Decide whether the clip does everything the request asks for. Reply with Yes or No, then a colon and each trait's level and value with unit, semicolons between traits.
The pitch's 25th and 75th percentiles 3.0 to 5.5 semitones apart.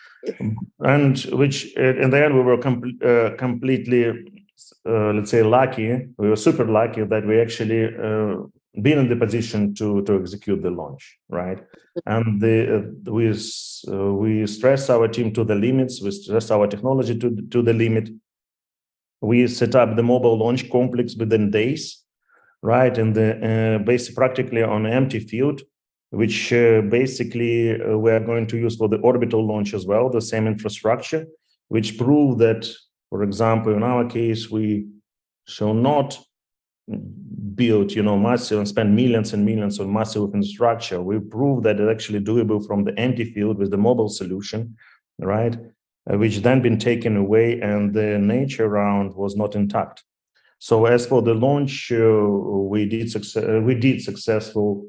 No: narrow, 2.5 semitones